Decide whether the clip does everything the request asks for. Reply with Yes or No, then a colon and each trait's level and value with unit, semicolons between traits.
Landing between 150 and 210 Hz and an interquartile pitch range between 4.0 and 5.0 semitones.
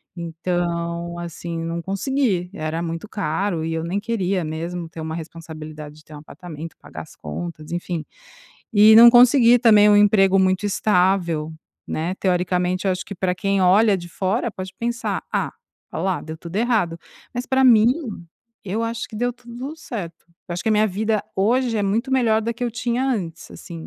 Yes: medium, 185 Hz; average, 4.7 semitones